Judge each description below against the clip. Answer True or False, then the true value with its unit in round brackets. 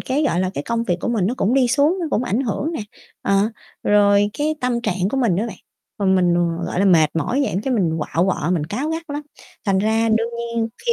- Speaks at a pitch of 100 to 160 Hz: False (225 Hz)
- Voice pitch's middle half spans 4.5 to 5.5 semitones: True (5.1 semitones)